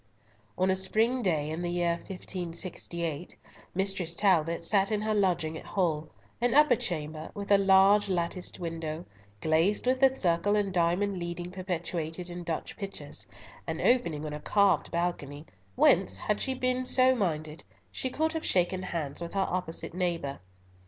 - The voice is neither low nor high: Yes, medium, 180 Hz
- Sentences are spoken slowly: No, average, 160 wpm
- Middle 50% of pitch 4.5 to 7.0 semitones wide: No, average, 3.4 semitones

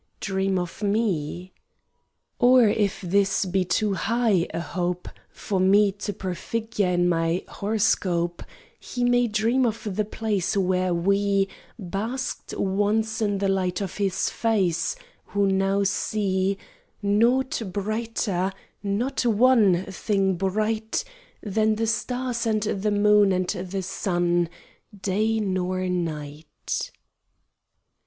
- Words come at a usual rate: No, slow, 120 wpm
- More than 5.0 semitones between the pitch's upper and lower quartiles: No, average, 2.8 semitones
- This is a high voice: Yes, high, 200 Hz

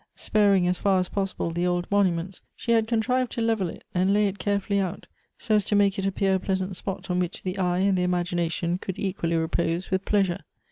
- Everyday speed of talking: No, fast, 225 wpm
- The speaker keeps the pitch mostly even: Yes, narrow, 2.2 semitones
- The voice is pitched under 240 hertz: Yes, high, 190 Hz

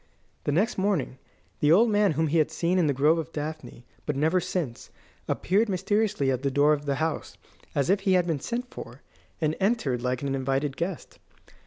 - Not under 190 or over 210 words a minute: Yes, average, 200 wpm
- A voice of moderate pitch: Yes, medium, 155 Hz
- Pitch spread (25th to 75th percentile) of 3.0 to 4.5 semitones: No, average, 5.3 semitones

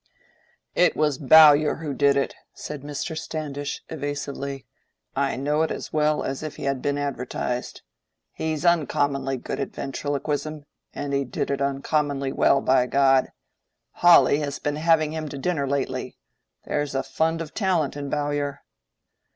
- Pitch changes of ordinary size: No, narrow, 1.8 semitones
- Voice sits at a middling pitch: Yes, medium, 145 Hz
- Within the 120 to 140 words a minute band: No, average, 150 wpm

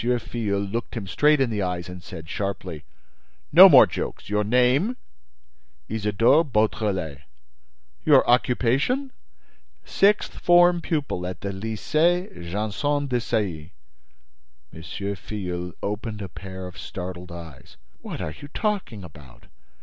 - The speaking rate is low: Yes, slow, 125 wpm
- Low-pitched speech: Yes, low, 105 Hz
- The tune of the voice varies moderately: No, wide, 6.5 semitones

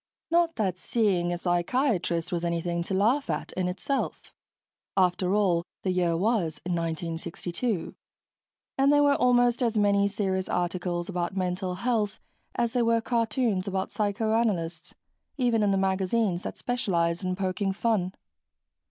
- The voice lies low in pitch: No, high, 190 Hz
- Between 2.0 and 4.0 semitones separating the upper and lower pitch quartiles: No, average, 4.5 semitones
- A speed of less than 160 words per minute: Yes, average, 140 wpm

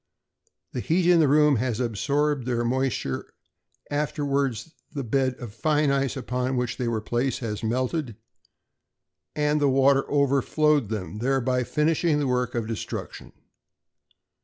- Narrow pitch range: No, average, 3.5 semitones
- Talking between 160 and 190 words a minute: No, slow, 135 wpm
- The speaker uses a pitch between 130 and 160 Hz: Yes, low, 135 Hz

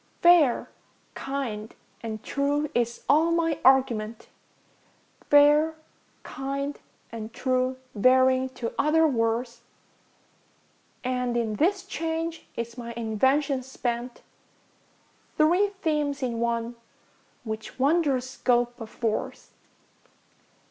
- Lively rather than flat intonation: No, average, 3.9 semitones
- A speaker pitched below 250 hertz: No, very high, 260 Hz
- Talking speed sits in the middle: No, slow, 95 wpm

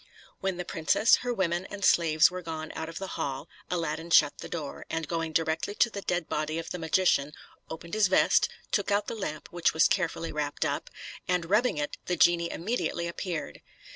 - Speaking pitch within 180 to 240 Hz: No, medium, 170 Hz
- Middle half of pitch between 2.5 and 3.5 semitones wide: Yes, average, 2.9 semitones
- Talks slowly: No, average, 200 wpm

